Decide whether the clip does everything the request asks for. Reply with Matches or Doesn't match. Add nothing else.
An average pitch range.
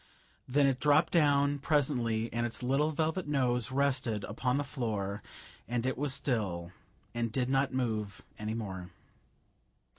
Matches